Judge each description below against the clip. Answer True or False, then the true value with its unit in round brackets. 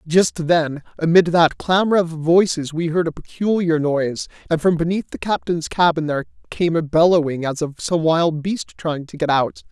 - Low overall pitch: False (165 Hz)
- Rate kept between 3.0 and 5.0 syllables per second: True (4.9 syllables/s)